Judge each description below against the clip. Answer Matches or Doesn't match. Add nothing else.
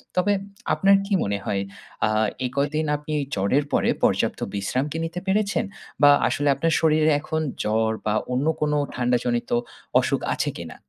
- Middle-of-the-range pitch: Matches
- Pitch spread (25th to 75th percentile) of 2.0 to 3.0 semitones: Doesn't match